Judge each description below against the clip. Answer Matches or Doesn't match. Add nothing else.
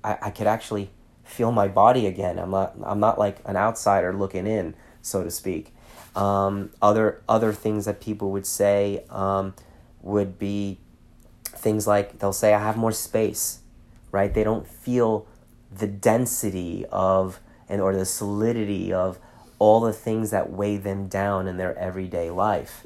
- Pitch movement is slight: Matches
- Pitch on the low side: Matches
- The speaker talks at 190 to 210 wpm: Doesn't match